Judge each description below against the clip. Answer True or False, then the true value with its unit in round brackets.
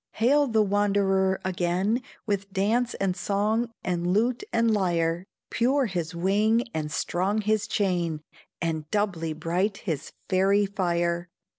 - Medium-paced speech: False (130 wpm)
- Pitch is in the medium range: False (195 Hz)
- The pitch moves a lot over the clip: False (3.6 semitones)